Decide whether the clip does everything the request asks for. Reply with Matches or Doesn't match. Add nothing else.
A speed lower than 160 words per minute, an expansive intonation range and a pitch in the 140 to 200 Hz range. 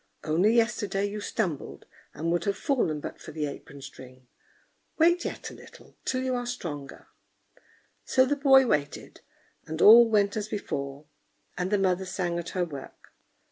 Doesn't match